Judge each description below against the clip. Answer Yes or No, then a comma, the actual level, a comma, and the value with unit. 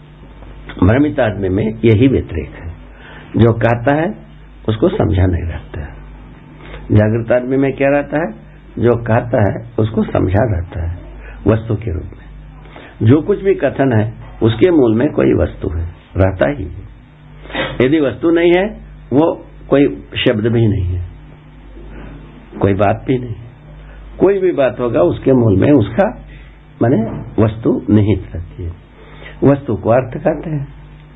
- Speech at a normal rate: Yes, average, 145 wpm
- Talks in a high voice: No, low, 115 Hz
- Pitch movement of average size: No, wide, 6.5 semitones